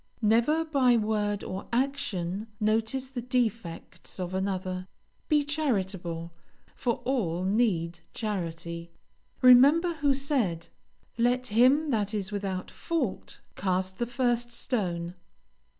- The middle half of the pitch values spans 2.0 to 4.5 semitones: No, wide, 5.4 semitones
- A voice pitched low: No, high, 220 Hz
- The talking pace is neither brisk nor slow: No, slow, 110 wpm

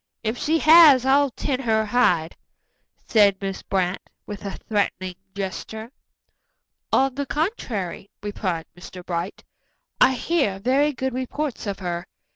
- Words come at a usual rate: No, slow, 130 wpm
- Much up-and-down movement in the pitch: Yes, wide, 5.8 semitones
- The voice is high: Yes, high, 220 Hz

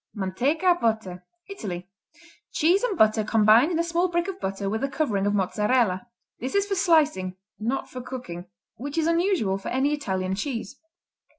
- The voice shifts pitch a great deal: Yes, wide, 8.8 semitones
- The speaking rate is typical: Yes, average, 170 wpm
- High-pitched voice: Yes, very high, 250 Hz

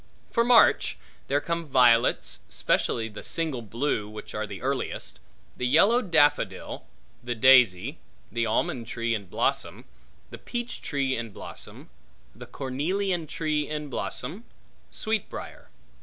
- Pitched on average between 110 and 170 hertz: Yes, low, 135 Hz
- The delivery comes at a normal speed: No, slow, 130 wpm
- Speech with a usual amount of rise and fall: No, wide, 6.0 semitones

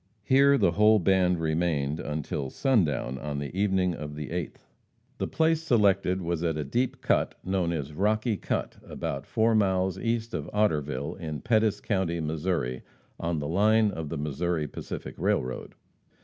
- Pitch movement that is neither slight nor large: No, wide, 5.8 semitones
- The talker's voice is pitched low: Yes, very low, 90 Hz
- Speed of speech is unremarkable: Yes, average, 160 wpm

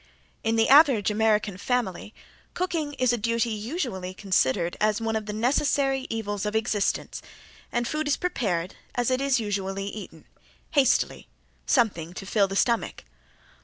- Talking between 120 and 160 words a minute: Yes, average, 150 wpm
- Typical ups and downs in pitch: Yes, average, 4.2 semitones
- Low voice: No, high, 220 Hz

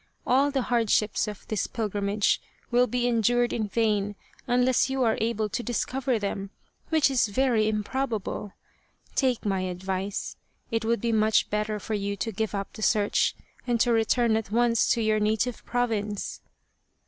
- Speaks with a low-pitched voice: No, high, 220 Hz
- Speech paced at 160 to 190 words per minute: Yes, average, 170 wpm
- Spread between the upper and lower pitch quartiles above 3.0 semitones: No, average, 2.7 semitones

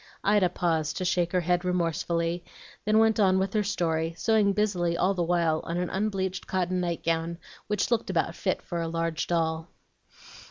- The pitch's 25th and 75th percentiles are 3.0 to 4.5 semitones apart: No, narrow, 2.6 semitones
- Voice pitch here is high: No, medium, 175 Hz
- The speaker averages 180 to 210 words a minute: Yes, average, 185 wpm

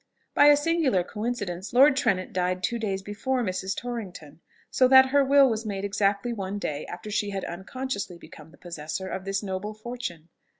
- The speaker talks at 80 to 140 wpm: No, average, 180 wpm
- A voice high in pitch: Yes, high, 205 Hz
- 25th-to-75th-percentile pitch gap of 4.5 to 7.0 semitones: Yes, average, 4.9 semitones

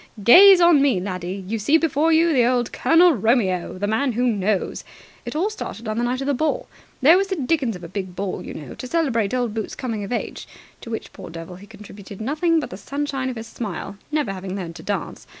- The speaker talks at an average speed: No, fast, 230 wpm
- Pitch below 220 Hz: No, high, 235 Hz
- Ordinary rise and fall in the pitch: No, wide, 6.8 semitones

